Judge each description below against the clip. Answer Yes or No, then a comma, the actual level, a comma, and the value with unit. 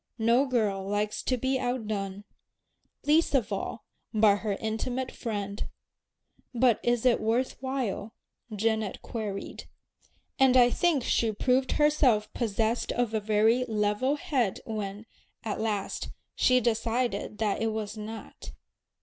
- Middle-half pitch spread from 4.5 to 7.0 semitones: No, average, 3.2 semitones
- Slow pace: Yes, slow, 130 wpm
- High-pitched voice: Yes, high, 225 Hz